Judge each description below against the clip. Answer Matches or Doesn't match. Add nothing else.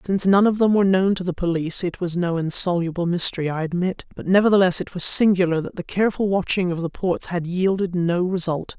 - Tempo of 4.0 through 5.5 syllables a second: Doesn't match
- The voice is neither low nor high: Matches